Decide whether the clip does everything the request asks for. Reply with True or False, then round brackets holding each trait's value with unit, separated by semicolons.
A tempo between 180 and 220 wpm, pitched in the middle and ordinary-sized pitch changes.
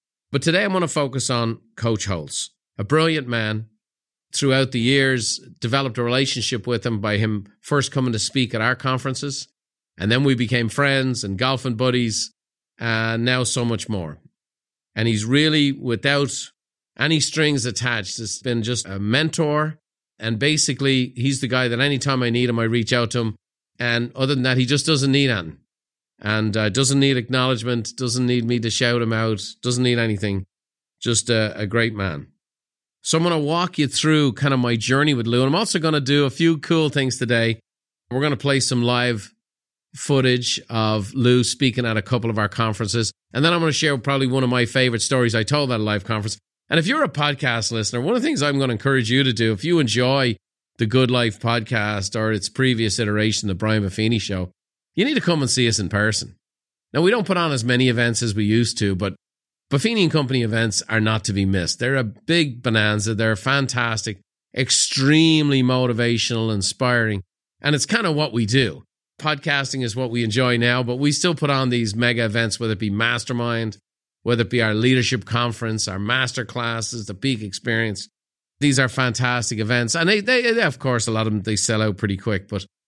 False (205 wpm; 120 Hz; 3.5 semitones)